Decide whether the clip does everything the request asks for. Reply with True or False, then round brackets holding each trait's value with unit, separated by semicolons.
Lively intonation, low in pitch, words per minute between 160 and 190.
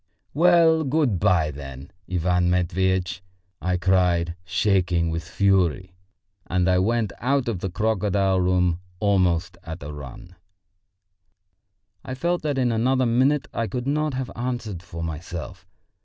False (5.7 semitones; 95 Hz; 135 wpm)